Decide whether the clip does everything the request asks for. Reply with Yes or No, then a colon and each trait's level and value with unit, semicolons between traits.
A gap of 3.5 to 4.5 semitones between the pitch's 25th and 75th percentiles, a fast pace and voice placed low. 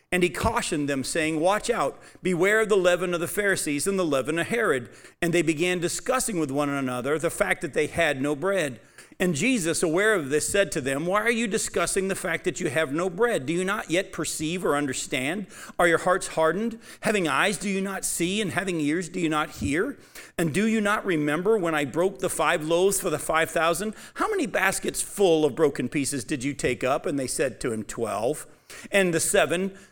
No: average, 3.8 semitones; fast, 225 wpm; medium, 175 Hz